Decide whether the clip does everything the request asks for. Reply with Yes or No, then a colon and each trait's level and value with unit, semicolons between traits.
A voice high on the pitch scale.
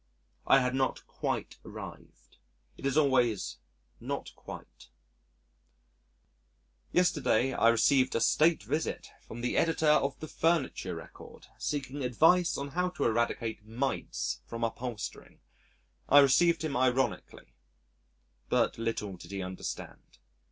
No: low, 130 Hz